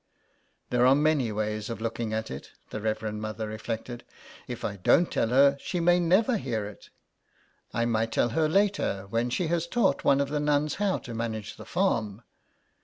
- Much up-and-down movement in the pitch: Yes, wide, 5.9 semitones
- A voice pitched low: Yes, low, 120 Hz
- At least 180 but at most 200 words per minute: Yes, average, 190 wpm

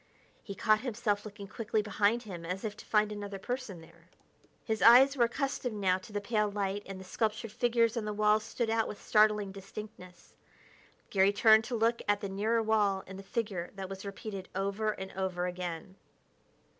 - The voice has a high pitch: Yes, high, 210 Hz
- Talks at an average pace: Yes, average, 190 wpm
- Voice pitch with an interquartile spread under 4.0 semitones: Yes, narrow, 2.4 semitones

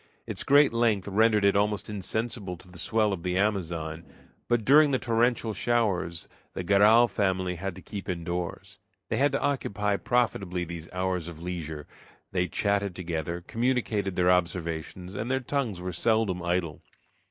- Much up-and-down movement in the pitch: No, average, 4.2 semitones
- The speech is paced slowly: No, average, 160 wpm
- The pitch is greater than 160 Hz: No, very low, 95 Hz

